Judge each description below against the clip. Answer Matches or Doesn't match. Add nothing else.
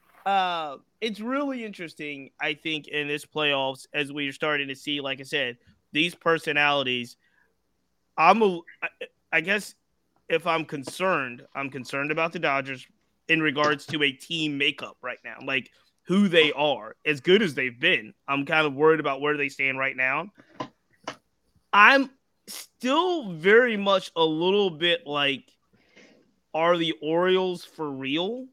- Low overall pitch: Doesn't match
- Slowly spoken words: Doesn't match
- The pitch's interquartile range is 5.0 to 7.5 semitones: Doesn't match